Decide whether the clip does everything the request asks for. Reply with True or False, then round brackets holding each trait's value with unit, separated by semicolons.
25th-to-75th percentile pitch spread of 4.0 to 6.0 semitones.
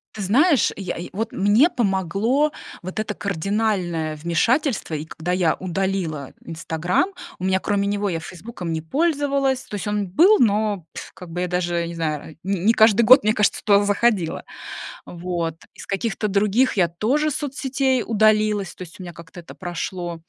True (4.5 semitones)